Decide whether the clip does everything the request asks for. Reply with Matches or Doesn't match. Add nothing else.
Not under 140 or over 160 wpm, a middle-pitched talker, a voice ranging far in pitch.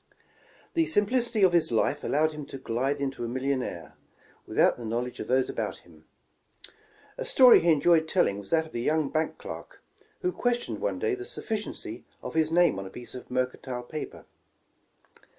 Doesn't match